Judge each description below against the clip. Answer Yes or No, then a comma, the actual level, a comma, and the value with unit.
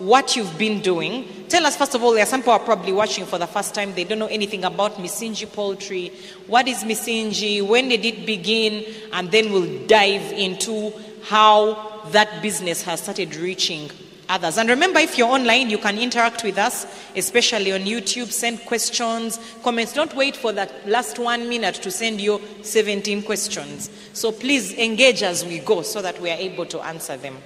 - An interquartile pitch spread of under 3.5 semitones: Yes, average, 3.0 semitones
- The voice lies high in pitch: Yes, high, 215 Hz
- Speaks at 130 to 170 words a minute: No, average, 195 wpm